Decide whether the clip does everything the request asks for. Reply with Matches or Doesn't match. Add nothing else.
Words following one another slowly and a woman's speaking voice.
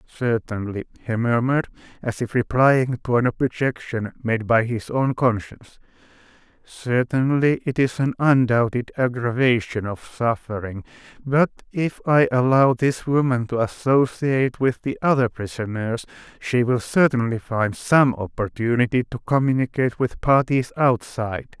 Doesn't match